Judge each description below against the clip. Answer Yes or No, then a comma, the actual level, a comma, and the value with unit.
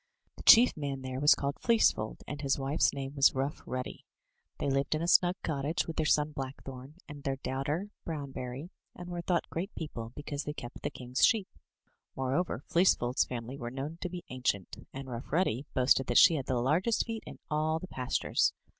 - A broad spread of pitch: No, average, 3.7 semitones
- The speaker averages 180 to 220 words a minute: Yes, average, 200 wpm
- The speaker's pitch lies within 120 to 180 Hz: Yes, medium, 140 Hz